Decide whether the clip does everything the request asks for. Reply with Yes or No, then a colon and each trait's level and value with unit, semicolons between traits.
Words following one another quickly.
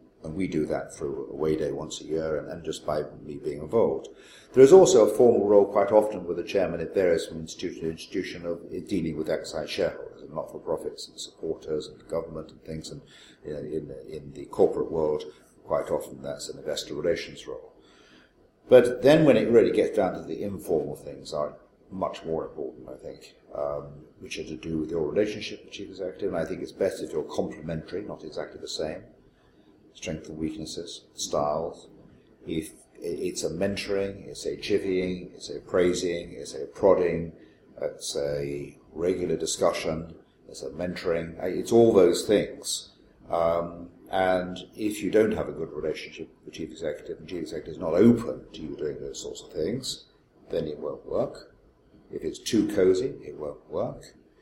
No: average, 185 wpm